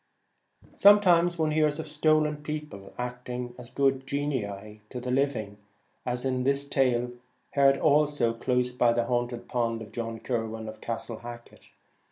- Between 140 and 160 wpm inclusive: Yes, average, 150 wpm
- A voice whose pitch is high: No, low, 125 Hz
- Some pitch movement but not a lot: Yes, average, 3.8 semitones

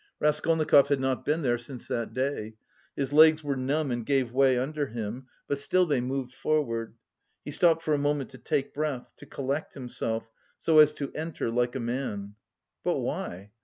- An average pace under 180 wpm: No, average, 185 wpm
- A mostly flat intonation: No, average, 3.5 semitones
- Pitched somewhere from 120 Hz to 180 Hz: Yes, low, 135 Hz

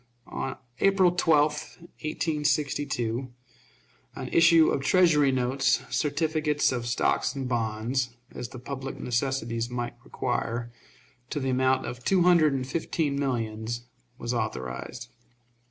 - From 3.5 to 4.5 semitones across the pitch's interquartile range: Yes, average, 3.9 semitones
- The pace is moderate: No, slow, 120 wpm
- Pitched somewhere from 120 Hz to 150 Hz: Yes, low, 135 Hz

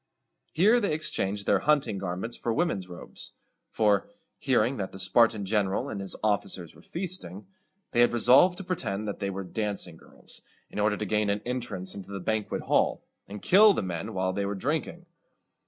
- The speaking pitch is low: Yes, low, 105 Hz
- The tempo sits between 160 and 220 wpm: Yes, average, 185 wpm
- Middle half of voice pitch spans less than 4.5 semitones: No, average, 4.8 semitones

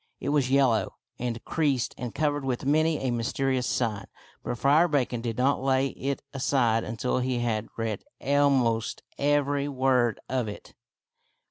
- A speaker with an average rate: Yes, average, 150 wpm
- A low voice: Yes, low, 130 Hz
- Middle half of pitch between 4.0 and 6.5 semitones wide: No, average, 3.0 semitones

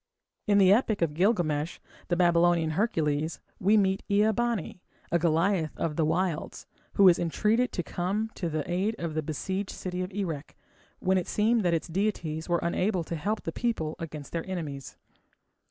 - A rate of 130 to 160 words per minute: No, average, 180 wpm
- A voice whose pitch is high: No, medium, 175 Hz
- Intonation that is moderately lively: Yes, average, 3.8 semitones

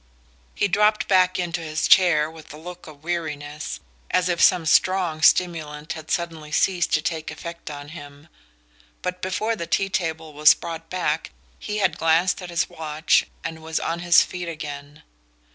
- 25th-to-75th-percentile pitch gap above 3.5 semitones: No, average, 2.7 semitones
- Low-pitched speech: No, medium, 165 Hz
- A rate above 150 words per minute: Yes, average, 170 wpm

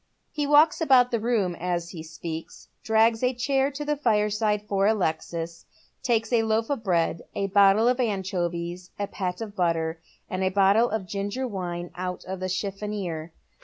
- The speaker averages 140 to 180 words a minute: Yes, average, 170 wpm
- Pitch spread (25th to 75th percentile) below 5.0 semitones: Yes, average, 4.2 semitones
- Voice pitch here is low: No, high, 200 Hz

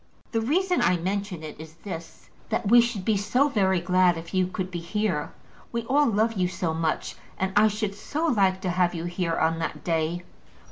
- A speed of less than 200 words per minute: No, fast, 205 wpm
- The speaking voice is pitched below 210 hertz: Yes, high, 190 Hz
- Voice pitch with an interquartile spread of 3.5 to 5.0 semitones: Yes, average, 4.0 semitones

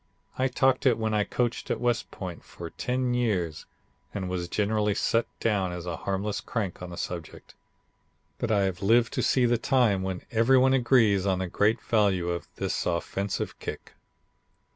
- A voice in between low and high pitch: No, low, 105 Hz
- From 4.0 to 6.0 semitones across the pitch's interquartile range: Yes, average, 4.6 semitones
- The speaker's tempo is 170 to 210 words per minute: Yes, average, 180 wpm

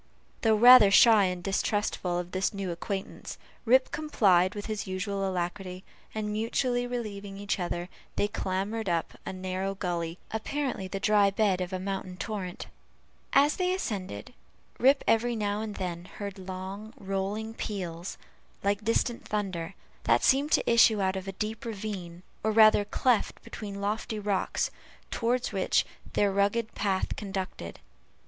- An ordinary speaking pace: Yes, average, 150 wpm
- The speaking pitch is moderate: No, high, 200 Hz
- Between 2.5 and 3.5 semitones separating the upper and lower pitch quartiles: Yes, average, 2.8 semitones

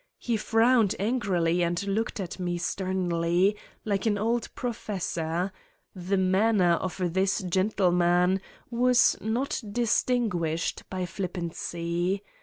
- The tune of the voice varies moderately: Yes, average, 3.7 semitones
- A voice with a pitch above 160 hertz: Yes, high, 190 Hz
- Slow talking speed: Yes, slow, 110 wpm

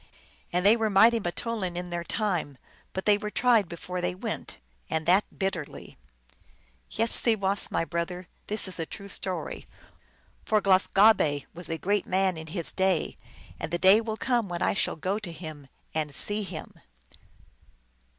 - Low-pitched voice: No, medium, 185 Hz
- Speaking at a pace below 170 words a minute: No, average, 175 wpm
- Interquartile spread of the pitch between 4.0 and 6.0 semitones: No, average, 3.4 semitones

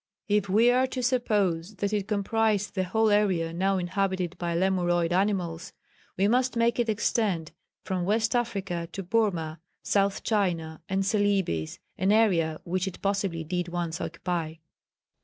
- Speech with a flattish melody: No, average, 3.4 semitones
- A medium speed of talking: Yes, average, 150 wpm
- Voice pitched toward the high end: Yes, high, 195 Hz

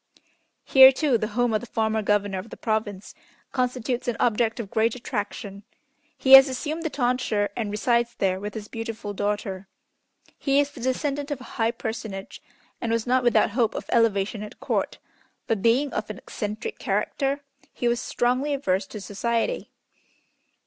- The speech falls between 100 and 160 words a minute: No, average, 170 wpm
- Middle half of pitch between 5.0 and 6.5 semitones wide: No, average, 3.4 semitones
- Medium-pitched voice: No, high, 230 Hz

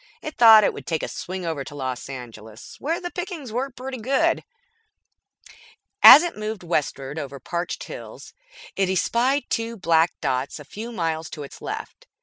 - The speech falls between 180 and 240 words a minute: No, average, 170 wpm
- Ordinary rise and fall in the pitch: No, wide, 8.7 semitones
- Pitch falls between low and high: Yes, medium, 180 Hz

